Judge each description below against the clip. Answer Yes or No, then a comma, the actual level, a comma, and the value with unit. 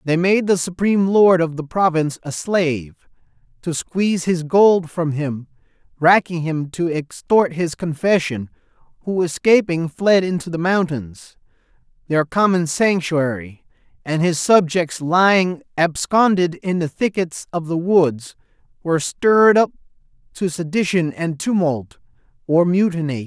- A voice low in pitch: No, medium, 170 Hz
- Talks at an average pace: No, slow, 130 wpm